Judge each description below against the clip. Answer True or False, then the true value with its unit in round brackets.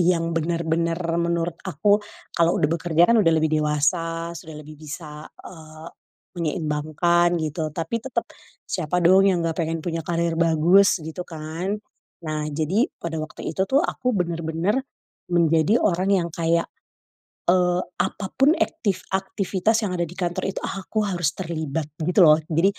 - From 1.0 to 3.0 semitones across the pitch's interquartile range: True (2.5 semitones)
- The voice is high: False (170 Hz)